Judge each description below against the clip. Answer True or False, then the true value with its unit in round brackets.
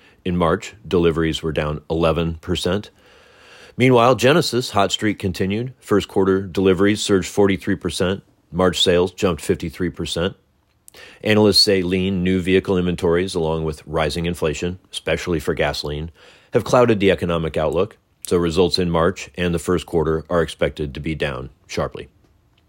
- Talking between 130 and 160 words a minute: True (140 wpm)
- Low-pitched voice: True (90 Hz)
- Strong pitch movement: False (2.8 semitones)